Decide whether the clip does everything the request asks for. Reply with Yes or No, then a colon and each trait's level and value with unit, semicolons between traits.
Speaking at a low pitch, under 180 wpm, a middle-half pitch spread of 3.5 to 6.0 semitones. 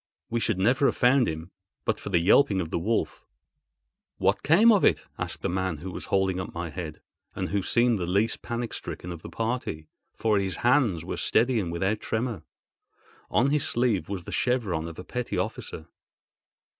No: low, 100 Hz; average, 195 wpm; wide, 5.6 semitones